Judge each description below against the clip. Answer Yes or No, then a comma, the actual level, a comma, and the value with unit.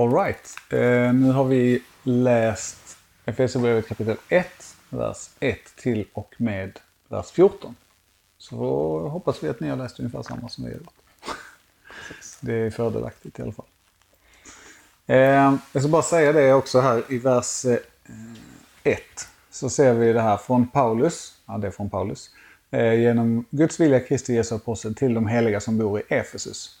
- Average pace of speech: Yes, average, 165 wpm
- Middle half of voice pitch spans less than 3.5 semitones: Yes, average, 2.7 semitones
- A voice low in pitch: Yes, low, 115 Hz